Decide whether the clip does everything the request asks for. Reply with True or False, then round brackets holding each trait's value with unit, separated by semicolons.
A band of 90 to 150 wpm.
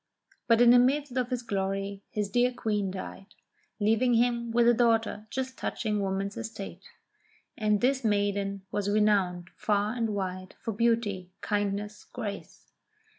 True (145 wpm)